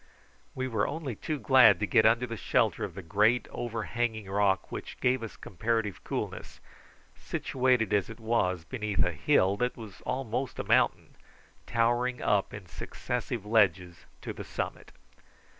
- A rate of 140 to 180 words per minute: Yes, average, 155 wpm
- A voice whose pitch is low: Yes, low, 110 Hz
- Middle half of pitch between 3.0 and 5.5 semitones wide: Yes, average, 3.3 semitones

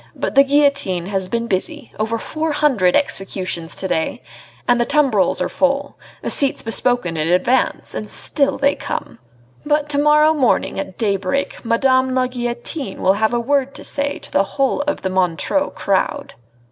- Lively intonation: Yes, wide, 6.5 semitones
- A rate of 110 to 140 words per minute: No, average, 170 wpm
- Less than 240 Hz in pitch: No, high, 245 Hz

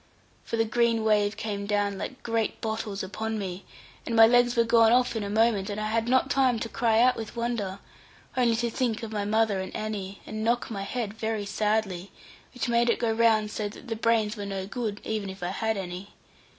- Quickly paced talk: Yes, fast, 215 wpm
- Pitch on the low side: No, high, 220 Hz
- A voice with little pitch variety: Yes, narrow, 2.2 semitones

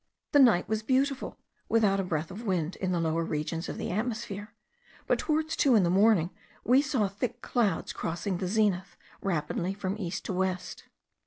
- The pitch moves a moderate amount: Yes, average, 4.3 semitones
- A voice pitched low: No, high, 195 Hz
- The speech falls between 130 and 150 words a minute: No, average, 180 wpm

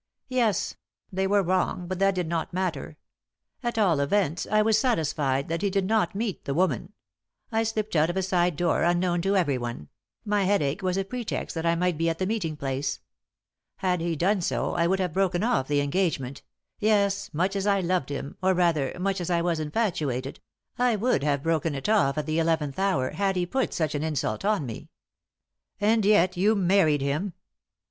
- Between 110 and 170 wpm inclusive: No, average, 200 wpm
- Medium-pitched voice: Yes, medium, 180 Hz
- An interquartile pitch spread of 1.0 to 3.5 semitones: No, average, 4.3 semitones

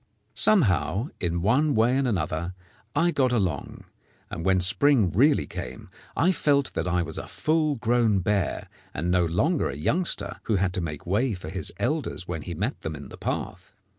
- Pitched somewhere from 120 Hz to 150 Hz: No, low, 100 Hz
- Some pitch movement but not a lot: No, wide, 7.9 semitones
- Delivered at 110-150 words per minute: No, average, 185 wpm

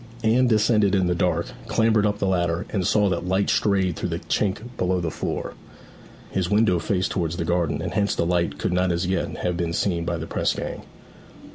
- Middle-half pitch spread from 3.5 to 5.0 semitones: No, average, 3.0 semitones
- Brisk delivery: Yes, fast, 215 wpm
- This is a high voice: No, very low, 90 Hz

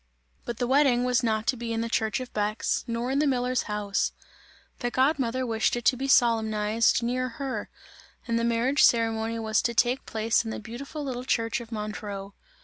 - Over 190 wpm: Yes, average, 200 wpm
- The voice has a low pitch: No, high, 235 Hz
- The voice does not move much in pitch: Yes, narrow, 2.3 semitones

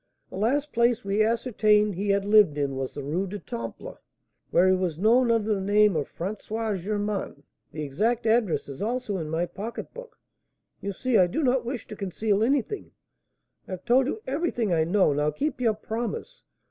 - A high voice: Yes, high, 210 Hz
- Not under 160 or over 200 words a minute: Yes, average, 185 wpm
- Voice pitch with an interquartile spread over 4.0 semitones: Yes, average, 4.5 semitones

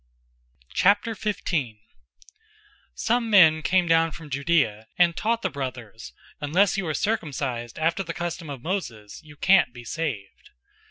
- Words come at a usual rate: No, slow, 130 wpm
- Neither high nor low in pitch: Yes, medium, 160 Hz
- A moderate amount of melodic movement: No, wide, 6.3 semitones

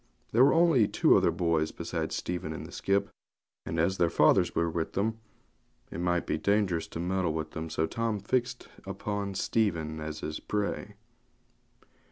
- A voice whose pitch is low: Yes, very low, 90 Hz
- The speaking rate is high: No, average, 170 wpm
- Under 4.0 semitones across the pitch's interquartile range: No, average, 4.3 semitones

